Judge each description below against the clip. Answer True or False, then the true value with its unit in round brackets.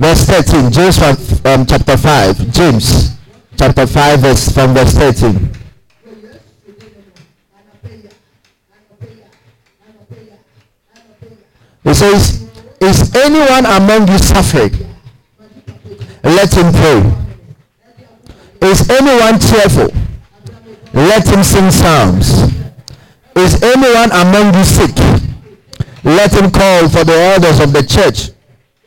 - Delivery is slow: True (90 wpm)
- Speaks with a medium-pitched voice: True (145 Hz)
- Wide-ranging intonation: True (8.5 semitones)